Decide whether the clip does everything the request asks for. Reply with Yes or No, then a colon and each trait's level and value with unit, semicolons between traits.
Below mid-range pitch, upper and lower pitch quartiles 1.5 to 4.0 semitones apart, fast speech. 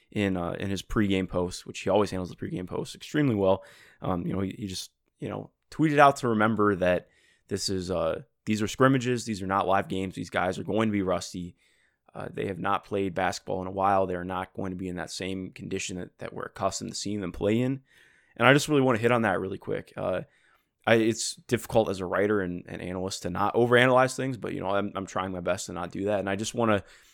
Yes: low, 100 Hz; average, 3.6 semitones; fast, 260 wpm